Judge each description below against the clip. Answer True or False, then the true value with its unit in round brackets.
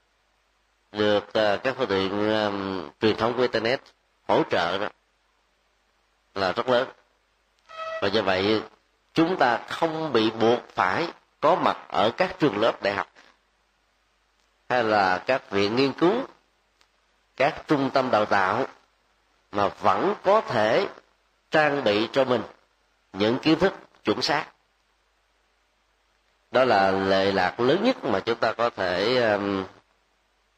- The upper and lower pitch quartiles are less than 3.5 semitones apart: False (5.3 semitones)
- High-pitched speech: False (110 Hz)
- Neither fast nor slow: False (135 wpm)